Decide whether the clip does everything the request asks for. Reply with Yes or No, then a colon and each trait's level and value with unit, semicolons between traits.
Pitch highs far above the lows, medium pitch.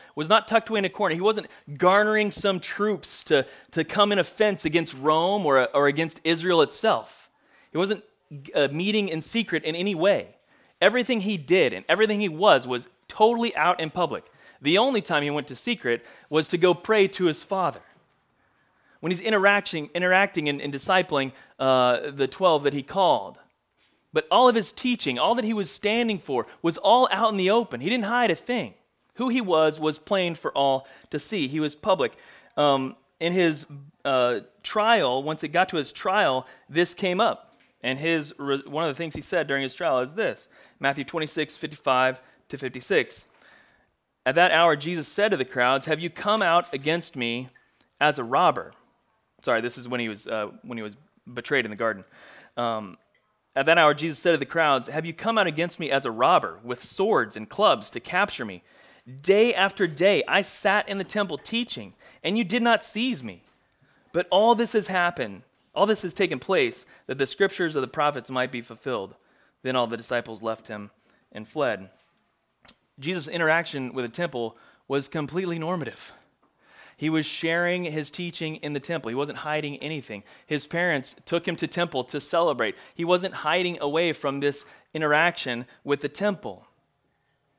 Yes: wide, 5.7 semitones; medium, 165 Hz